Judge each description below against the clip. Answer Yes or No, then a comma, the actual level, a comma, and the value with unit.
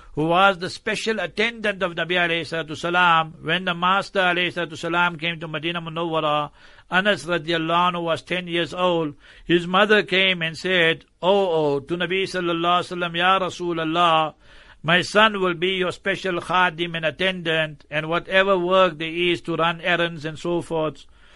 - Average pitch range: No, narrow, 2.0 semitones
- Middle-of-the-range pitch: Yes, medium, 175 Hz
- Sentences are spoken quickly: No, average, 155 wpm